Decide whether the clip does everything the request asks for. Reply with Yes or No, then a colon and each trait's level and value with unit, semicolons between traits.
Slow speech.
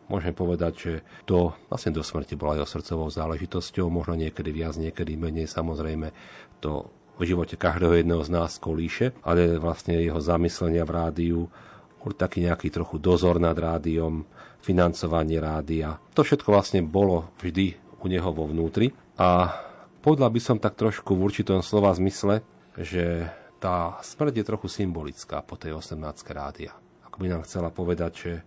No: average, 155 wpm